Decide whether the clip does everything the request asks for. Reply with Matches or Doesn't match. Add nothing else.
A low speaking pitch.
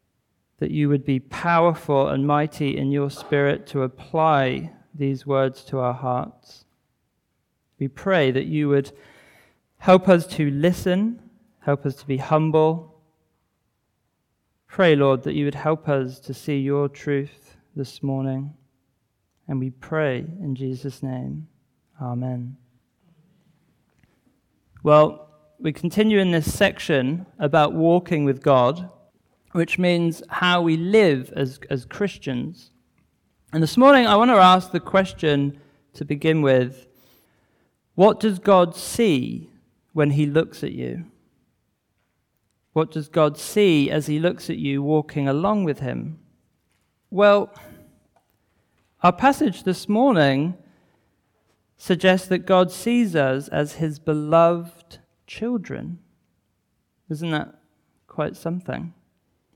Doesn't match